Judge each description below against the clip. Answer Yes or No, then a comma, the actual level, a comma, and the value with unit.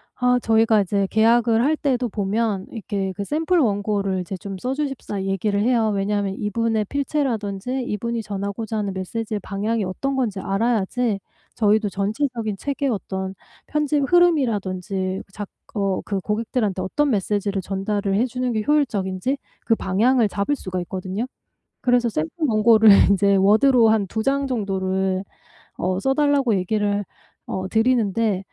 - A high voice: Yes, high, 215 Hz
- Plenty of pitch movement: No, average, 3.9 semitones